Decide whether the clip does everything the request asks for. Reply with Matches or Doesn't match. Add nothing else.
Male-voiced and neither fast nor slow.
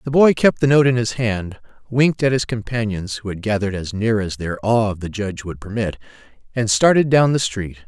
Doesn't match